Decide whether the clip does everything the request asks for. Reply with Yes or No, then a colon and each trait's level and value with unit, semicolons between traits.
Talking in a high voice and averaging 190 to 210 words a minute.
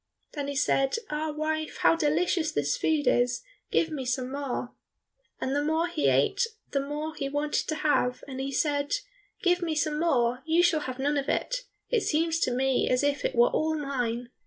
Yes: very high, 290 Hz; average, 200 wpm